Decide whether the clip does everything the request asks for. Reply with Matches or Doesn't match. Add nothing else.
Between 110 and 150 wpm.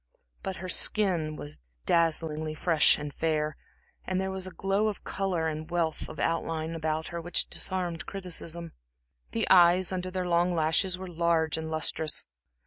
Doesn't match